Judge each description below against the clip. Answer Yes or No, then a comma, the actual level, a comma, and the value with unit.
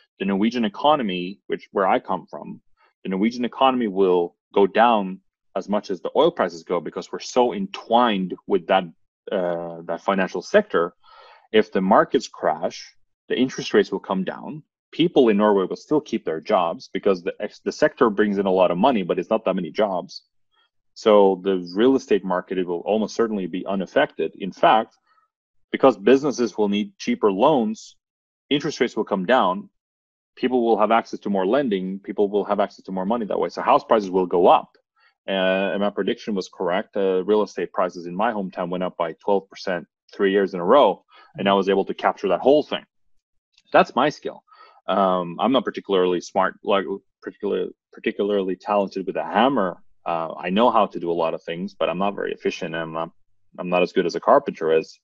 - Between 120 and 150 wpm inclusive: No, average, 200 wpm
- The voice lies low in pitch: Yes, low, 100 Hz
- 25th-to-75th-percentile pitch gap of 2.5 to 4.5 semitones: Yes, average, 3.1 semitones